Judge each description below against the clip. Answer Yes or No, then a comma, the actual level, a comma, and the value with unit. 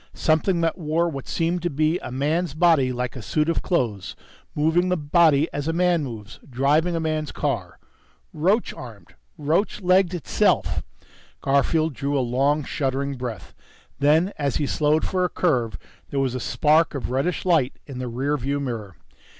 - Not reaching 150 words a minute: No, average, 175 wpm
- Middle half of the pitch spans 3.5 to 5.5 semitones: Yes, average, 3.9 semitones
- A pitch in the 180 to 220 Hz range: No, medium, 150 Hz